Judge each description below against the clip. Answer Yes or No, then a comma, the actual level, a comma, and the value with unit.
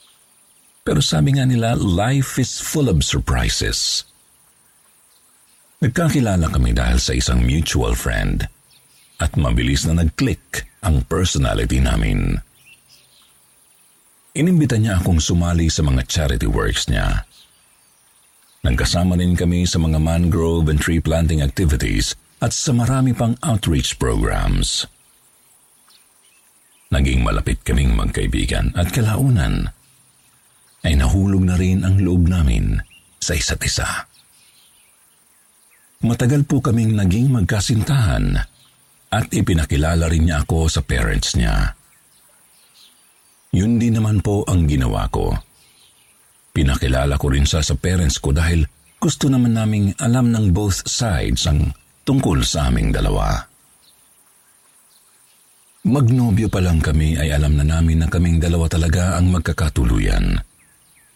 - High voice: No, very low, 85 Hz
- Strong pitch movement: Yes, wide, 6.2 semitones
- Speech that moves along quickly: No, average, 115 wpm